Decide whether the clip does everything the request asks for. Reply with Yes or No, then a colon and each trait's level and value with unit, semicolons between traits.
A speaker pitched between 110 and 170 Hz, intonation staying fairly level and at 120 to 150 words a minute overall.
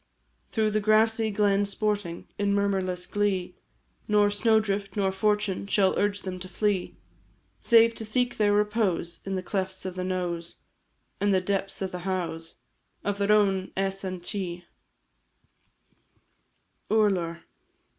No: high, 200 Hz; narrow, 2.1 semitones; average, 140 wpm